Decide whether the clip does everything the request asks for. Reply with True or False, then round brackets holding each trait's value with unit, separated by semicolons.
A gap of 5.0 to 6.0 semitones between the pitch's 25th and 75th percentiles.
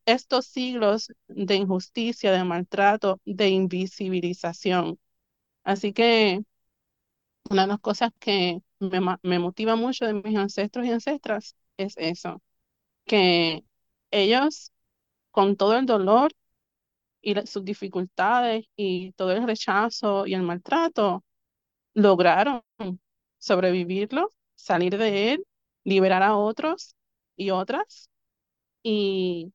False (3.3 semitones)